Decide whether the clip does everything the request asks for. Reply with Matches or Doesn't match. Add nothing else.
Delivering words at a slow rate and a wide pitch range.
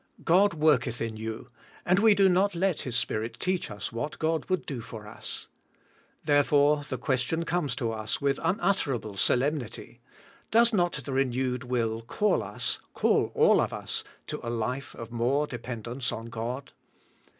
Doesn't match